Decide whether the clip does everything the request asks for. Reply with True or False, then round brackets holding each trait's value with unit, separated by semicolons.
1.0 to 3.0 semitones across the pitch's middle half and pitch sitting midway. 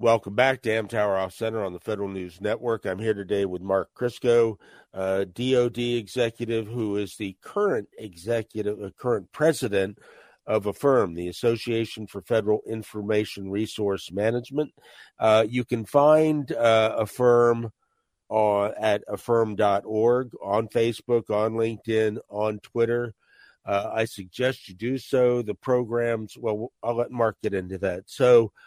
False (2.7 semitones; 110 Hz)